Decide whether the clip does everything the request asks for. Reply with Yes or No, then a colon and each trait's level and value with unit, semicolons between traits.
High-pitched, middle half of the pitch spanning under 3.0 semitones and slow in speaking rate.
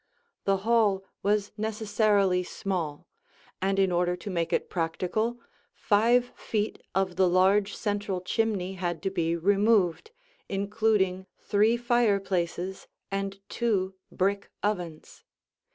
Yes: high, 195 Hz; narrow, 2.5 semitones; slow, 115 wpm